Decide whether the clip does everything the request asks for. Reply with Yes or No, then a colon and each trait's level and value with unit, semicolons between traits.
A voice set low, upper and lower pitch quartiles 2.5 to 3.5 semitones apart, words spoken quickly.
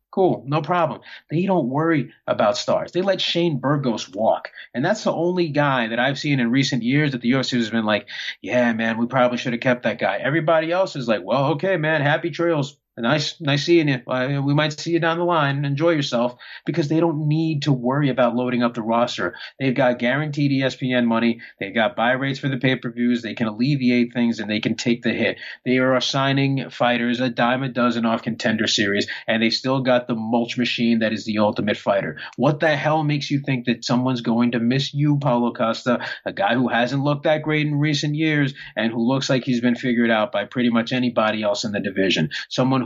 No: low, 130 Hz; average, 3.9 semitones; fast, 225 wpm